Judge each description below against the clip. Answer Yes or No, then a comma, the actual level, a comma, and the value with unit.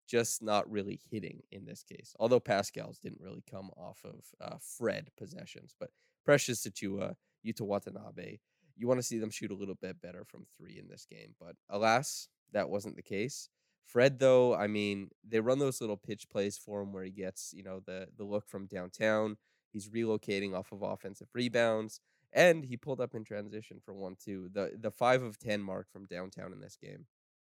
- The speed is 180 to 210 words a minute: Yes, average, 200 wpm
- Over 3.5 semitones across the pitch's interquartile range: No, average, 2.8 semitones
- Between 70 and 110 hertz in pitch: Yes, low, 105 Hz